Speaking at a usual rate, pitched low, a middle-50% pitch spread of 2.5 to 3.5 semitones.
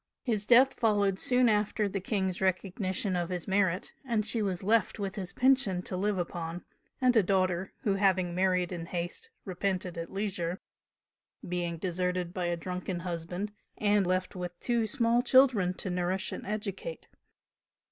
No: average, 160 wpm; high, 190 Hz; average, 2.8 semitones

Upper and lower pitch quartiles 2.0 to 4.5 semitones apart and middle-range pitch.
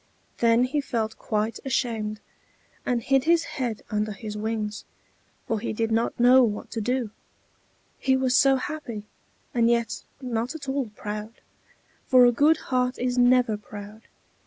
No: average, 2.9 semitones; high, 235 Hz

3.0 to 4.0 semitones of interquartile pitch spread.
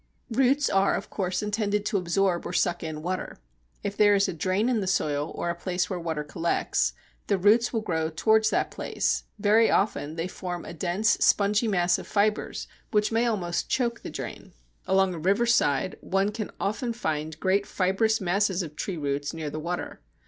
Yes: average, 3.6 semitones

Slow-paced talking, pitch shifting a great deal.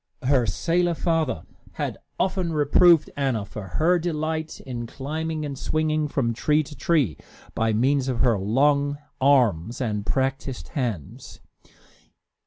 No: slow, 130 wpm; average, 5.0 semitones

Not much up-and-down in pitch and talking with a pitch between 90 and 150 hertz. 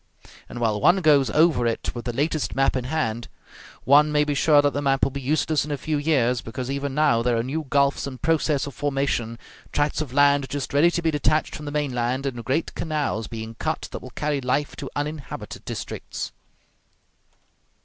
No: average, 3.1 semitones; medium, 140 Hz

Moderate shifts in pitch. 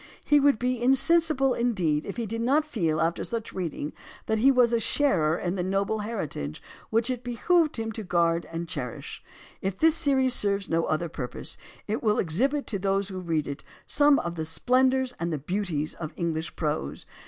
No: wide, 7.2 semitones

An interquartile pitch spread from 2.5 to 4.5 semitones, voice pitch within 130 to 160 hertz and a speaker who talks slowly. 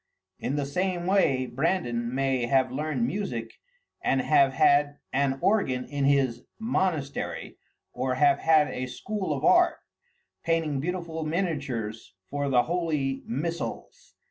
Yes: average, 4.2 semitones; medium, 140 Hz; slow, 130 wpm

